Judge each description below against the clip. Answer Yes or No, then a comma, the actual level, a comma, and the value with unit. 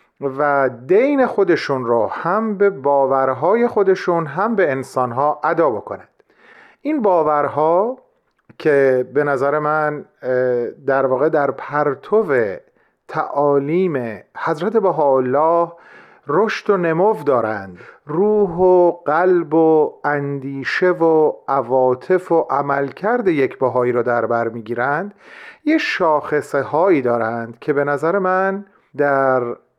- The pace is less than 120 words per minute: Yes, average, 110 wpm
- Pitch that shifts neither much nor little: No, wide, 6.1 semitones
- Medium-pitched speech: Yes, medium, 150 Hz